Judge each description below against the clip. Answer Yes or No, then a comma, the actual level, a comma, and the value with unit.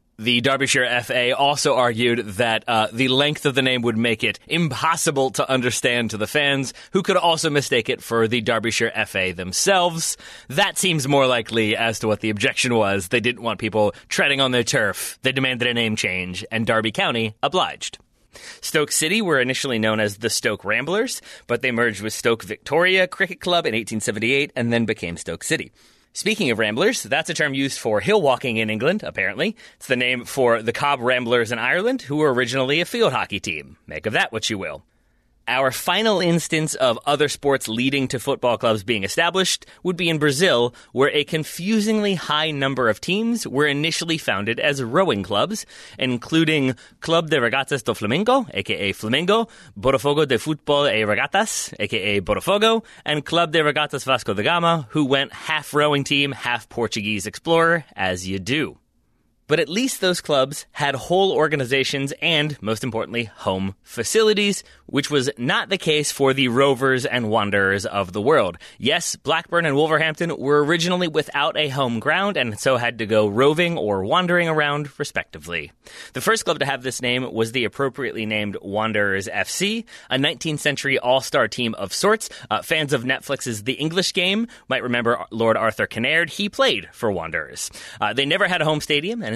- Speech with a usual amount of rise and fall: No, wide, 5.7 semitones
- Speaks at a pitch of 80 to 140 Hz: Yes, low, 135 Hz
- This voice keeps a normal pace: Yes, average, 180 wpm